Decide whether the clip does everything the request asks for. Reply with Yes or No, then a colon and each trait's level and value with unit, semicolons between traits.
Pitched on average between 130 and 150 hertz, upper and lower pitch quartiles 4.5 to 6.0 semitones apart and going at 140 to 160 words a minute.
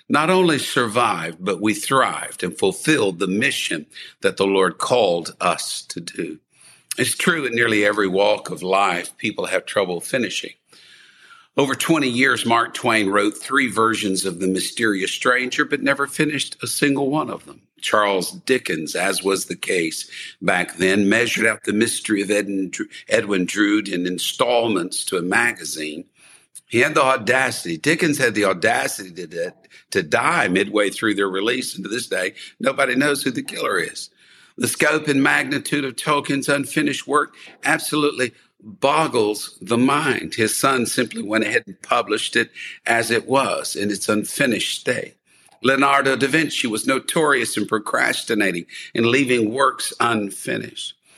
No: low, 120 Hz; wide, 5.6 semitones; average, 155 wpm